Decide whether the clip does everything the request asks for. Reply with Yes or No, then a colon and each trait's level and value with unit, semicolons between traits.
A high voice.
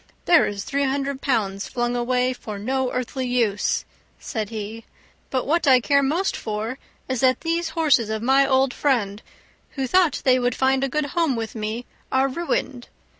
Yes: very high, 255 Hz